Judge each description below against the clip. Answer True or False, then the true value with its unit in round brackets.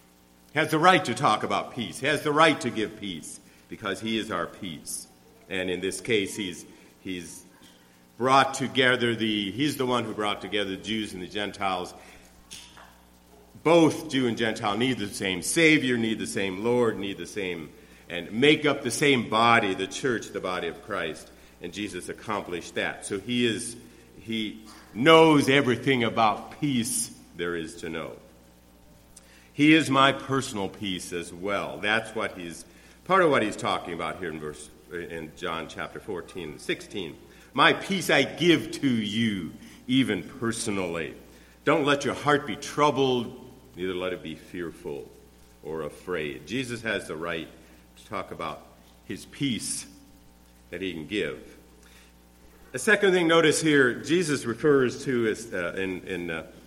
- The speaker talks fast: False (165 wpm)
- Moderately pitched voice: False (105 Hz)